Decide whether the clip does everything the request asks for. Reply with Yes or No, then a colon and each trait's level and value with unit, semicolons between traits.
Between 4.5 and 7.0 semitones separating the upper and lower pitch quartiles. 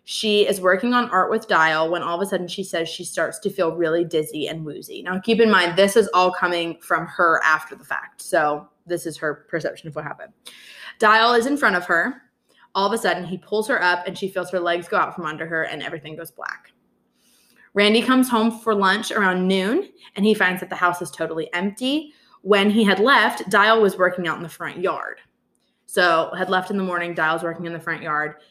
No: average, 3.9 semitones